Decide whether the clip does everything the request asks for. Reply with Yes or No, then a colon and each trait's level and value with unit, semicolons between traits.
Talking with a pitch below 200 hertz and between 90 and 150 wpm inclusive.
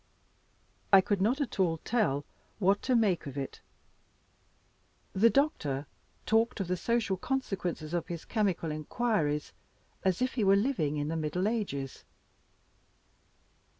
Yes: high, 190 Hz; slow, 135 wpm